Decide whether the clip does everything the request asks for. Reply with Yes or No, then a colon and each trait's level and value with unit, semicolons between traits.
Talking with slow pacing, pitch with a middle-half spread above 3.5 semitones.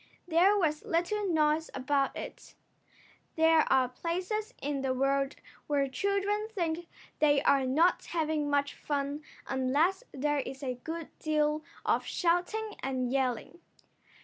Yes: slow, 130 wpm; average, 4.0 semitones